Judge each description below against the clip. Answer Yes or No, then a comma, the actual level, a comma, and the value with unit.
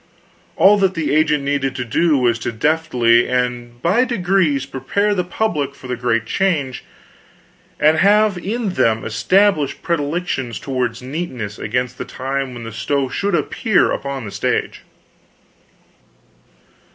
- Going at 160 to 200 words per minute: No, average, 140 wpm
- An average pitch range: No, wide, 6.3 semitones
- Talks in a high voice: No, medium, 140 Hz